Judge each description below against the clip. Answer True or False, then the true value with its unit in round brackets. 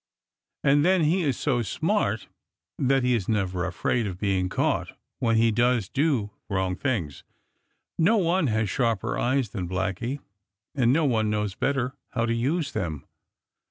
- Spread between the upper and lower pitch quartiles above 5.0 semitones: True (5.6 semitones)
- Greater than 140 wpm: True (160 wpm)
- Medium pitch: False (115 Hz)